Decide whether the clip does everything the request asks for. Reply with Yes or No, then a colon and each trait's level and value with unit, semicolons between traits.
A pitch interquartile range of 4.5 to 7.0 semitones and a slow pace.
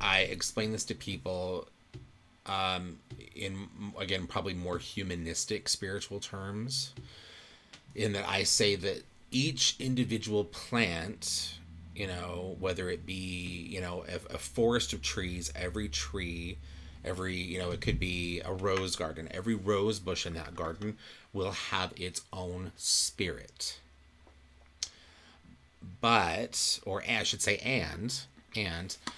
No: average, 3.7 semitones; slow, 130 wpm